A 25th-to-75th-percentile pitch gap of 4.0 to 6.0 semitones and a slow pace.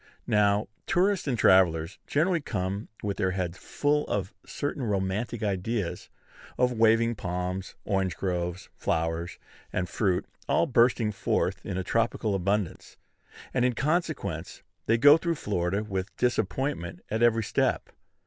Yes: average, 4.5 semitones; slow, 130 wpm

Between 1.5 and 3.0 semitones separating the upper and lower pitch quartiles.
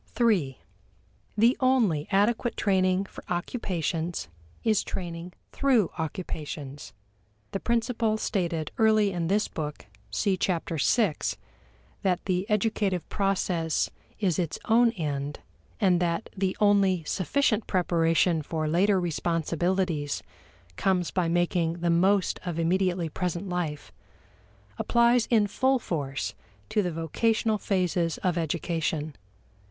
No: average, 3.9 semitones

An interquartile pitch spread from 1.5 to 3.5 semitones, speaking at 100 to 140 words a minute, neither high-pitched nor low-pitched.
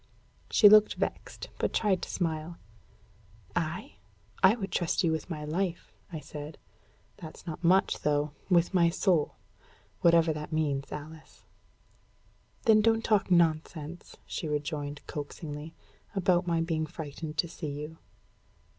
Yes: average, 2.8 semitones; slow, 135 wpm; medium, 165 Hz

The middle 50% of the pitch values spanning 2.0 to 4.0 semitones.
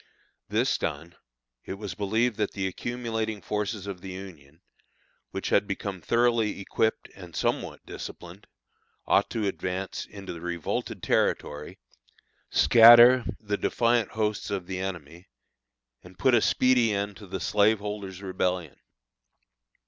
Yes: average, 3.2 semitones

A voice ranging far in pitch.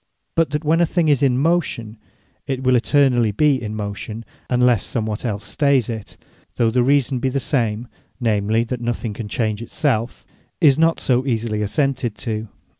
No: average, 4.0 semitones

